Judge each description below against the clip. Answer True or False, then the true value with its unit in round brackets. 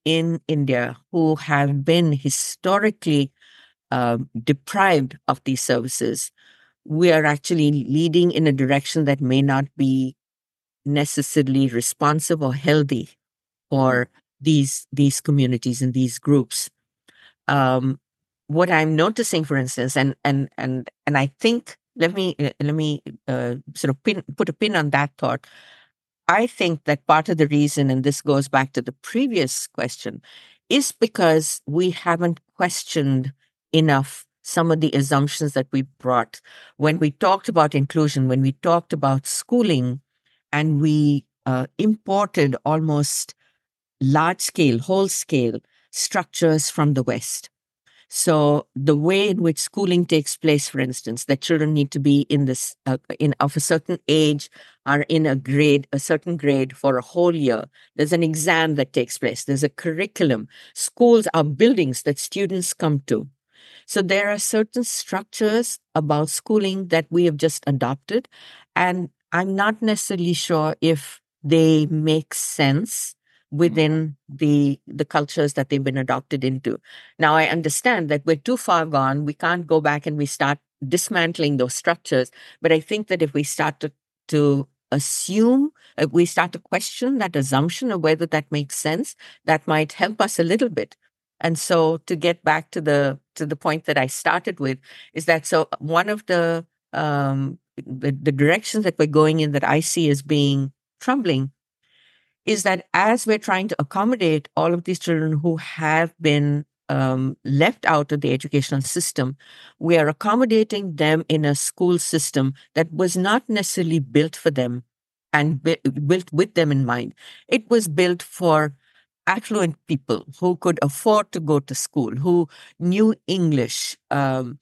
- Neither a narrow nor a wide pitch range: True (3.8 semitones)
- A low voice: False (155 Hz)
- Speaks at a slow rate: False (160 wpm)